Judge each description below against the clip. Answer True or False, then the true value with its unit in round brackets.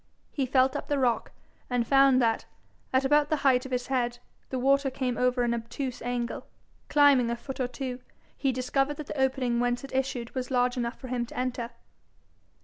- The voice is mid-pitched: False (255 Hz)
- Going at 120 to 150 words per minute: False (200 wpm)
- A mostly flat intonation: True (1.7 semitones)